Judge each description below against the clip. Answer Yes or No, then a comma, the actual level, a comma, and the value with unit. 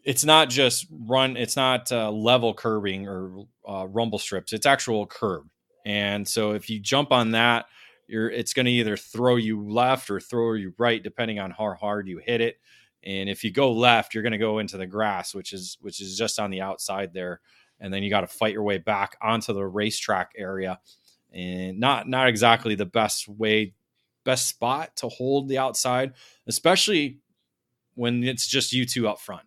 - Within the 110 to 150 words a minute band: No, average, 200 wpm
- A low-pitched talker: Yes, low, 110 Hz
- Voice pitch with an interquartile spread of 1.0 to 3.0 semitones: No, average, 3.6 semitones